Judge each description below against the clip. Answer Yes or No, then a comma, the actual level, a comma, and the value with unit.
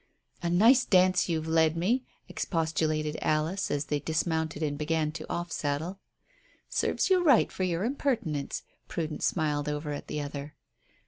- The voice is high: No, medium, 160 Hz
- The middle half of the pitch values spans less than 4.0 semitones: Yes, average, 3.2 semitones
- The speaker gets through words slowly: No, average, 150 wpm